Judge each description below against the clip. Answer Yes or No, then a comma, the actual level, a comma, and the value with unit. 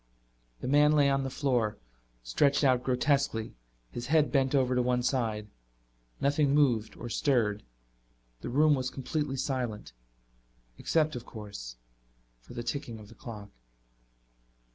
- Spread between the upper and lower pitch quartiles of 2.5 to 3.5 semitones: No, average, 3.9 semitones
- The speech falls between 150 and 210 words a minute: No, average, 140 wpm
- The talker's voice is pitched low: Yes, low, 130 Hz